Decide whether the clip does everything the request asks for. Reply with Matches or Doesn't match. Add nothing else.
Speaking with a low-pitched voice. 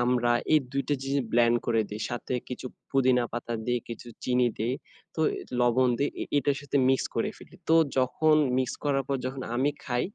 Matches